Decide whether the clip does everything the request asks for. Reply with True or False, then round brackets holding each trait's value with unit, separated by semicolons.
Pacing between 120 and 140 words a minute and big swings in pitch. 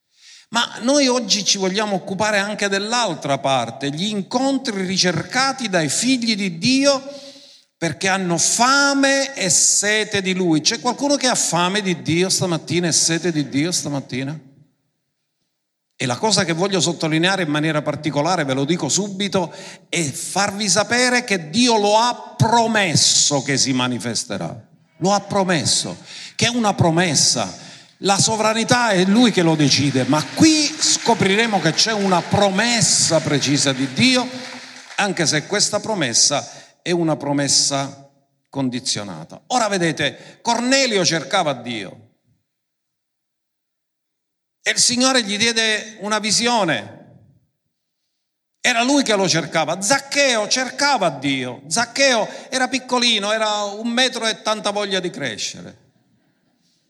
True (130 wpm; 7.1 semitones)